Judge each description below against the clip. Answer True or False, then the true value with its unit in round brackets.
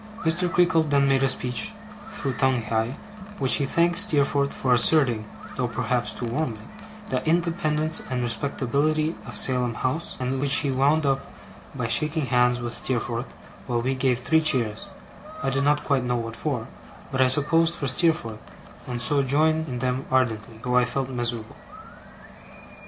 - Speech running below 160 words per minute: False (165 wpm)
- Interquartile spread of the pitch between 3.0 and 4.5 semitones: True (3.8 semitones)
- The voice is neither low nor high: False (130 Hz)